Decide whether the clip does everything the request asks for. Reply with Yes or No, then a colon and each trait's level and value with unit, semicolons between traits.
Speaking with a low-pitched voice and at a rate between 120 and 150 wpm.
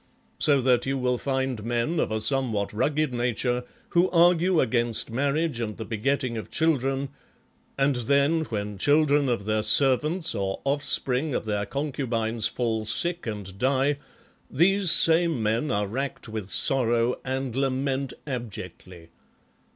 Yes: low, 130 Hz; average, 140 wpm